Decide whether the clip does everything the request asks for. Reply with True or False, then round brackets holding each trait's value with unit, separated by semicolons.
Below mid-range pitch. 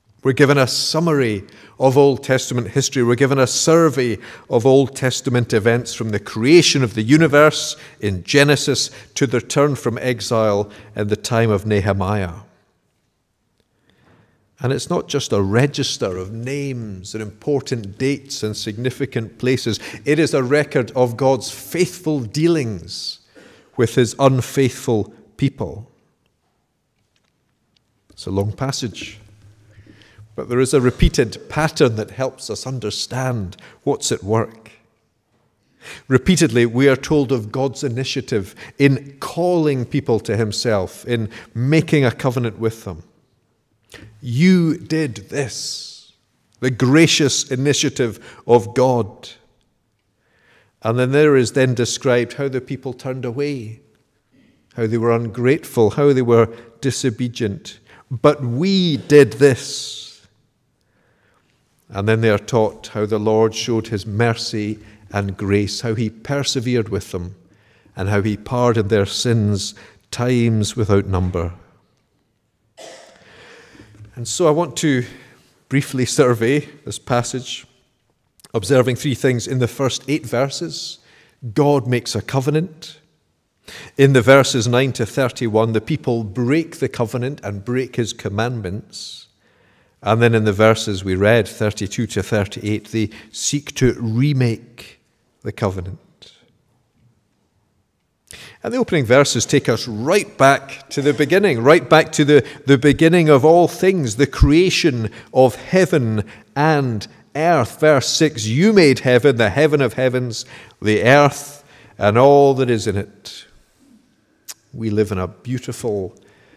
True (125 Hz)